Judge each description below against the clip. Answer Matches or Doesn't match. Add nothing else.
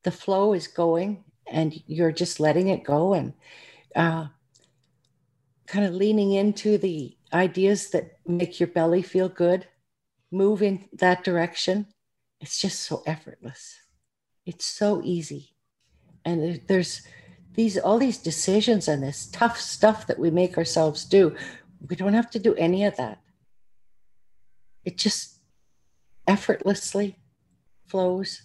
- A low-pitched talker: Doesn't match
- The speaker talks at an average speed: Doesn't match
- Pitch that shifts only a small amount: Doesn't match